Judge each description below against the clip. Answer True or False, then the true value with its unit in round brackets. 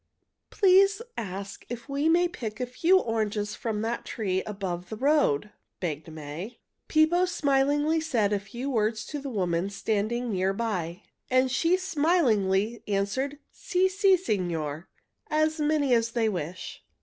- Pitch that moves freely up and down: True (7.4 semitones)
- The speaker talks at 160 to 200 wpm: False (150 wpm)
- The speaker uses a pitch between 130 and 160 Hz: False (230 Hz)